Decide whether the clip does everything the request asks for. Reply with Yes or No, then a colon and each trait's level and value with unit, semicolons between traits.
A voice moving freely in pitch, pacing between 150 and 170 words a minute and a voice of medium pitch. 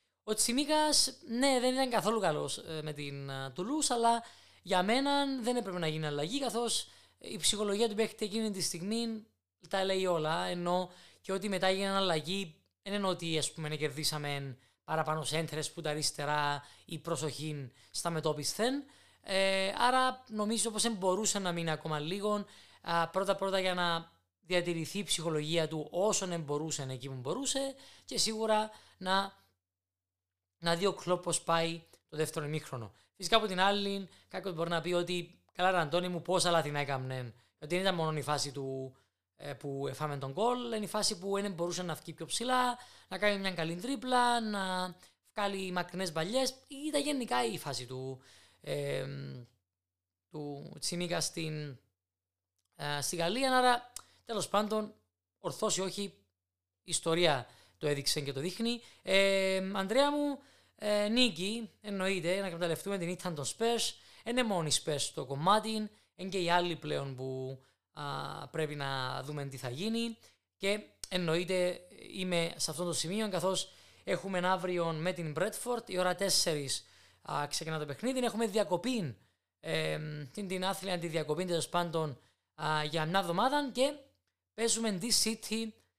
Yes: wide, 5.8 semitones; average, 155 wpm; medium, 180 Hz